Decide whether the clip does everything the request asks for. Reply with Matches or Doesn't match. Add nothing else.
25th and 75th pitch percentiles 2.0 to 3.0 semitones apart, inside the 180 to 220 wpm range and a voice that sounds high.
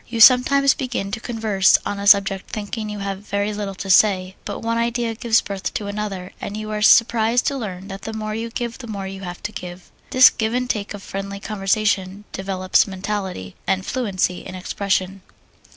Matches